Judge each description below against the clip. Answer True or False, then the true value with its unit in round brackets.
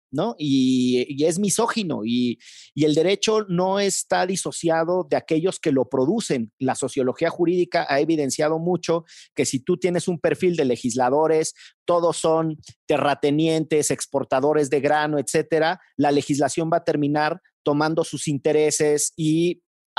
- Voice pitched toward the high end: False (155 Hz)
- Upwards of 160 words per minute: False (140 wpm)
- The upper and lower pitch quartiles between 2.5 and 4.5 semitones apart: True (3.0 semitones)